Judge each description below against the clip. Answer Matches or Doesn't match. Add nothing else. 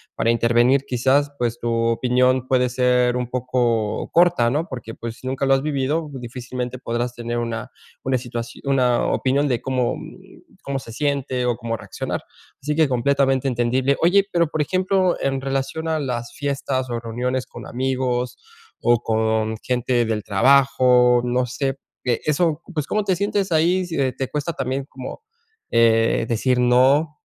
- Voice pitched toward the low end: Matches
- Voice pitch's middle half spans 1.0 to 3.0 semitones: Matches